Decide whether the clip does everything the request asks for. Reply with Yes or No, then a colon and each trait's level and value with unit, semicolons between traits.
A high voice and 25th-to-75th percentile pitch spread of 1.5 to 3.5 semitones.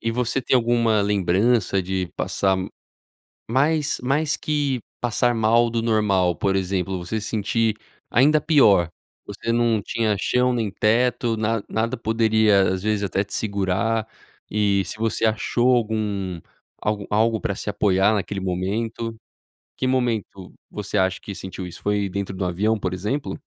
No: low, 110 Hz; average, 3.1 semitones